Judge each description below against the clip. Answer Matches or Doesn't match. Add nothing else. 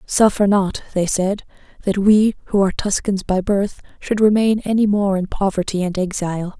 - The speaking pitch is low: Doesn't match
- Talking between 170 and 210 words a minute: Matches